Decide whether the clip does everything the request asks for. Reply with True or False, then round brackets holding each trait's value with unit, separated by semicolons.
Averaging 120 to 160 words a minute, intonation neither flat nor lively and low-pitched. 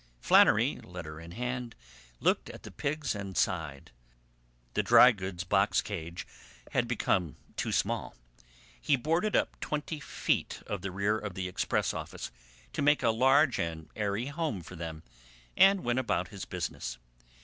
False (155 wpm; 6.6 semitones; 100 Hz)